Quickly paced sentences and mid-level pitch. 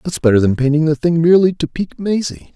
Yes: fast, 235 wpm; medium, 160 Hz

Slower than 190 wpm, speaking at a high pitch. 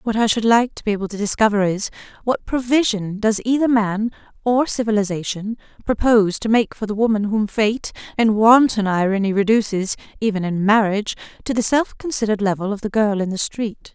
Yes: average, 180 wpm; high, 215 Hz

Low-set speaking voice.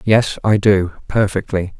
Yes: low, 100 Hz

